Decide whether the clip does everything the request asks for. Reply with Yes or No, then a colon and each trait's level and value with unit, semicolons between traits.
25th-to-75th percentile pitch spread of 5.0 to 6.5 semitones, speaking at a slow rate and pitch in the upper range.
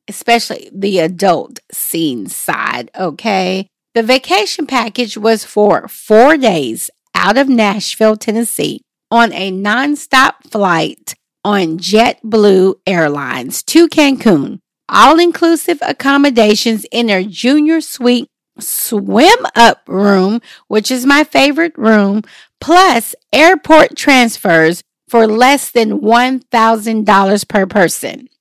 Yes: wide, 5.4 semitones; slow, 105 wpm; high, 230 Hz